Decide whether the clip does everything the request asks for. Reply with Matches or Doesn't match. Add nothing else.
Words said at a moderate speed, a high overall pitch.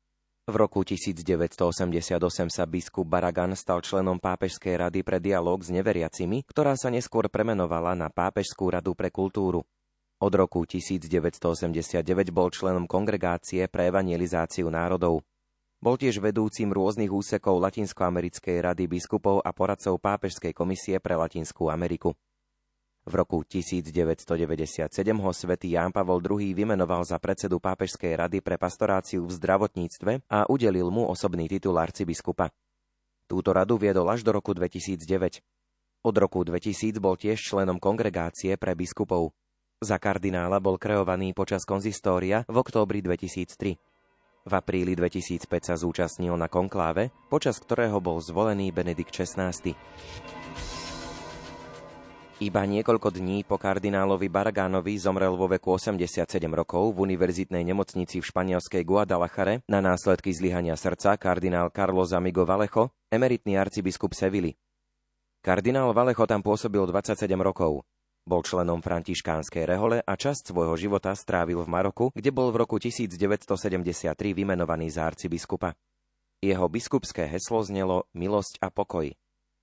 Doesn't match